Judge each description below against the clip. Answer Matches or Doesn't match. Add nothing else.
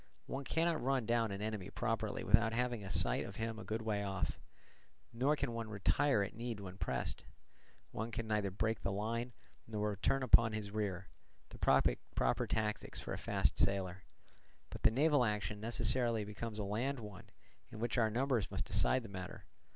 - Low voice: Matches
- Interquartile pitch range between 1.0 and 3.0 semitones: Matches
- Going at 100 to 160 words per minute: Doesn't match